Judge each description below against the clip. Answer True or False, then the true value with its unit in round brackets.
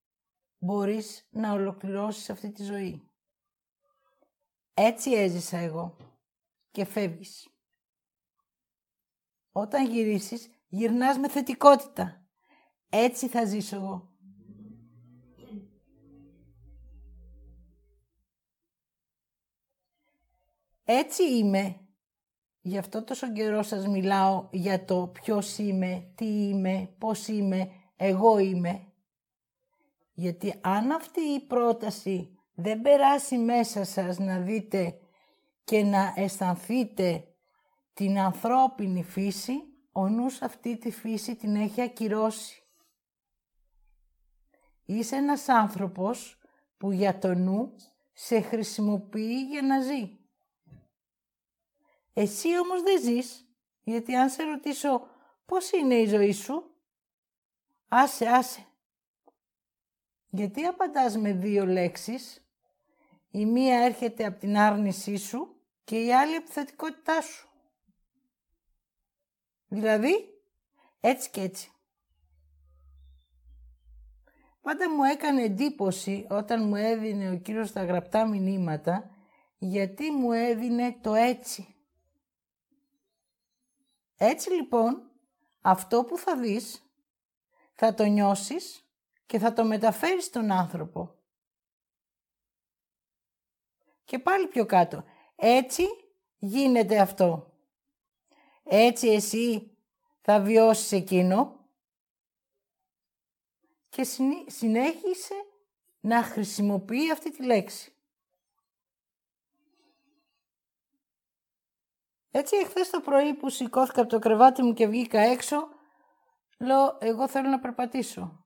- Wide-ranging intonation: True (5.7 semitones)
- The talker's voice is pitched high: True (225 Hz)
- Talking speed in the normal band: False (90 wpm)